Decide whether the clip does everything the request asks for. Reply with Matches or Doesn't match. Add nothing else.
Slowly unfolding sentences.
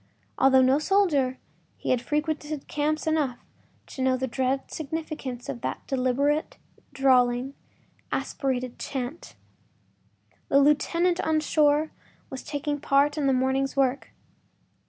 Matches